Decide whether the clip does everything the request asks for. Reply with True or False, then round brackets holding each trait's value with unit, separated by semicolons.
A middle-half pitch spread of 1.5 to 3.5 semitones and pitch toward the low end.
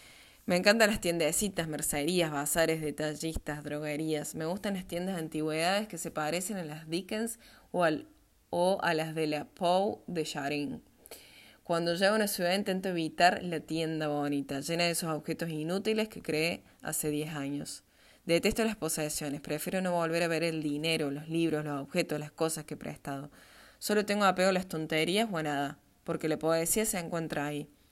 False (2.9 semitones; 160 Hz)